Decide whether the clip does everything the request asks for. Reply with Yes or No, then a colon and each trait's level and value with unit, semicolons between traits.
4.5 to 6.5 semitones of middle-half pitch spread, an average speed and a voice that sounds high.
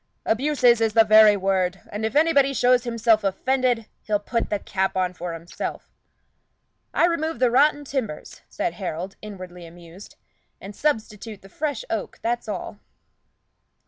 Yes: average, 4.8 semitones; average, 145 wpm; high, 220 Hz